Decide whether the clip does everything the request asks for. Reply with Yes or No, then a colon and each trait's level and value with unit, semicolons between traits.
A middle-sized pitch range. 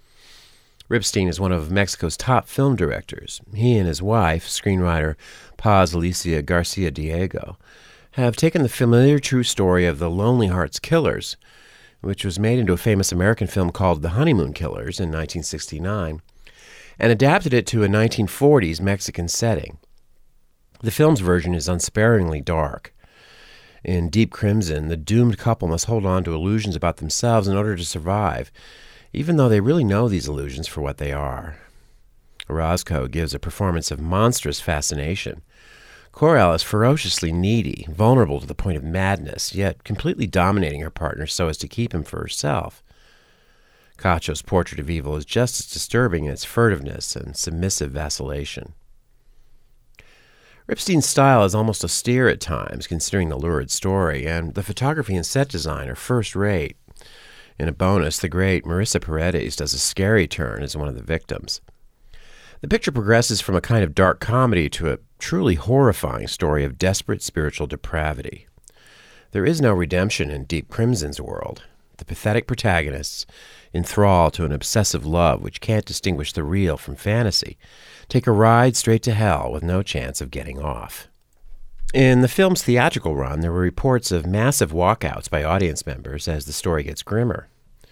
No: wide, 5.7 semitones